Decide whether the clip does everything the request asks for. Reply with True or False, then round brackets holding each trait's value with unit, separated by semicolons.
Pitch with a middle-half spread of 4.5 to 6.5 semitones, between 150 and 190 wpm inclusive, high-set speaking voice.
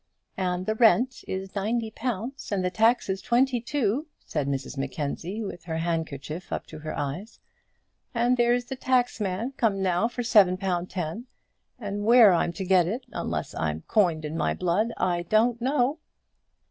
True (5.5 semitones; 160 wpm; 200 Hz)